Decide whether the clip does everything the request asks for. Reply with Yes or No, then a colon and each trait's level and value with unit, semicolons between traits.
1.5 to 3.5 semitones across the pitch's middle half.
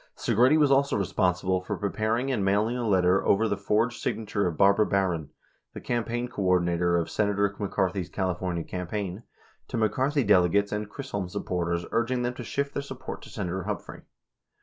No: average, 4.3 semitones